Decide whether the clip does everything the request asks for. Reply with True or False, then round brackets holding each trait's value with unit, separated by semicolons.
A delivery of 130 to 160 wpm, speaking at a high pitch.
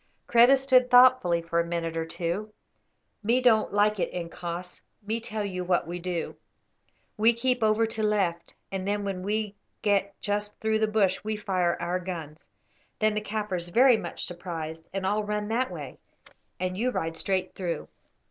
False (175 wpm; 200 Hz)